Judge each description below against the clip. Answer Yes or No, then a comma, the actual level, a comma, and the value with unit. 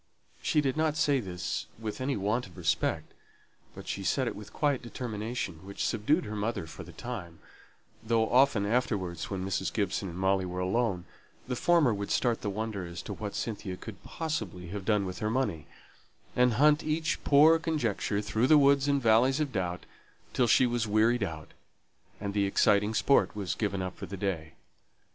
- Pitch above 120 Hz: No, low, 110 Hz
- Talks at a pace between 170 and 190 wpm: Yes, average, 185 wpm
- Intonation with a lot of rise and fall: No, average, 5.0 semitones